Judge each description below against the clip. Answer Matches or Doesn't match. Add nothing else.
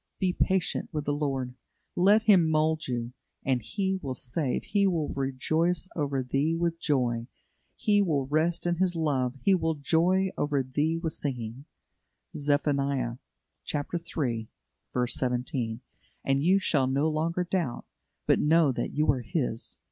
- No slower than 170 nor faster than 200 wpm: Doesn't match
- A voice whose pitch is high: Doesn't match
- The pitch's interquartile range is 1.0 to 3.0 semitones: Doesn't match